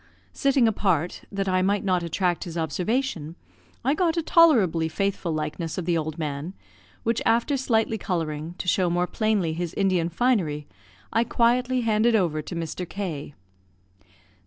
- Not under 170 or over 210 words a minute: No, average, 155 wpm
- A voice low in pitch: No, medium, 185 Hz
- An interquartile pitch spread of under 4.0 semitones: No, wide, 5.5 semitones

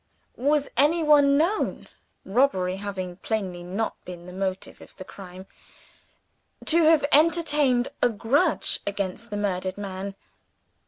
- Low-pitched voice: No, high, 205 Hz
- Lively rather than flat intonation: Yes, wide, 7.5 semitones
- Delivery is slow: Yes, slow, 120 wpm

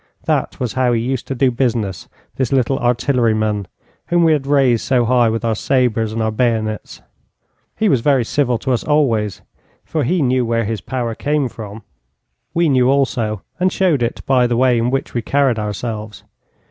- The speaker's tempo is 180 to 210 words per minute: Yes, average, 185 wpm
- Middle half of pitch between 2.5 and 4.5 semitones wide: Yes, average, 3.1 semitones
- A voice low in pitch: Yes, low, 125 Hz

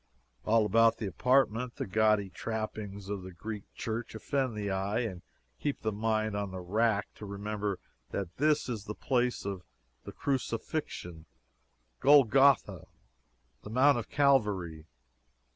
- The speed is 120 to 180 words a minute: Yes, average, 140 wpm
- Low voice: Yes, low, 110 Hz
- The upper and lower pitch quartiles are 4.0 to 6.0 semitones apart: No, average, 3.6 semitones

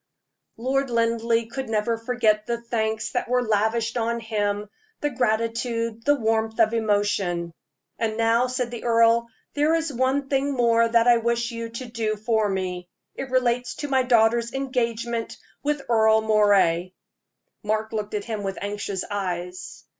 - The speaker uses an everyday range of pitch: No, narrow, 2.0 semitones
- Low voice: No, high, 230 Hz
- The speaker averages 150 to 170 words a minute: Yes, average, 155 wpm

